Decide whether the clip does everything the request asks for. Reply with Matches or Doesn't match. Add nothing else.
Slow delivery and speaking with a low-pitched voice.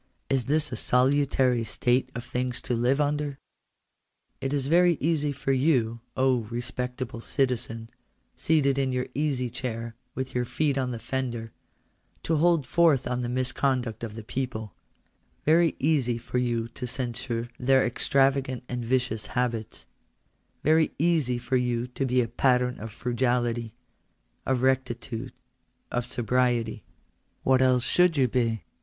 Doesn't match